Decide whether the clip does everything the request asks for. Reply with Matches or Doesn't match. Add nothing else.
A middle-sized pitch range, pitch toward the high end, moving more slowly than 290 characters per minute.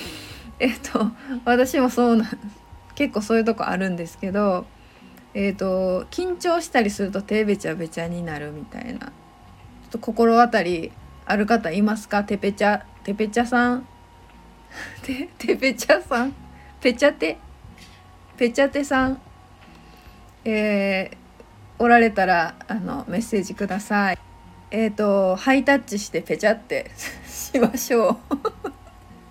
Matches